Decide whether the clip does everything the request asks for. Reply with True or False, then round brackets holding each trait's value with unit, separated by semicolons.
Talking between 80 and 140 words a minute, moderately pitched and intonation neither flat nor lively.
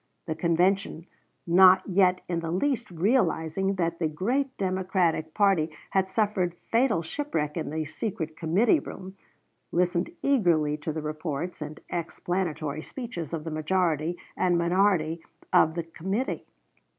True (135 wpm; 175 Hz; 3.2 semitones)